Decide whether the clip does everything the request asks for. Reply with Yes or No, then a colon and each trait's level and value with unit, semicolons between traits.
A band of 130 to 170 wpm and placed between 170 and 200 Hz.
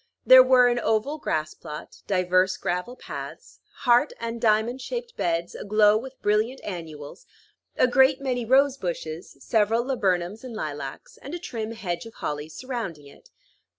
No: average, 150 wpm; high, 220 Hz